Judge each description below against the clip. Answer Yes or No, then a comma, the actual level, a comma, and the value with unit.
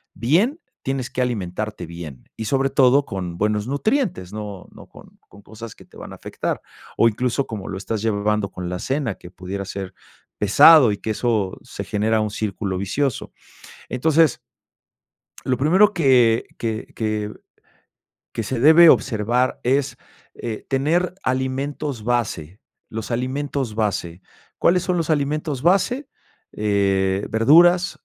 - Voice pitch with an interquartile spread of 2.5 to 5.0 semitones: No, wide, 5.5 semitones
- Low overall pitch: Yes, low, 115 Hz